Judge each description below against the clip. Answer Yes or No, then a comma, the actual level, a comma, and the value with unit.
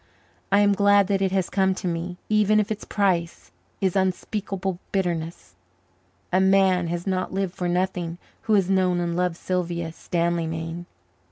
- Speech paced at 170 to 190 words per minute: No, average, 160 wpm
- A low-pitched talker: No, medium, 185 Hz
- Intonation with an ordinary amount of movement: No, narrow, 2.2 semitones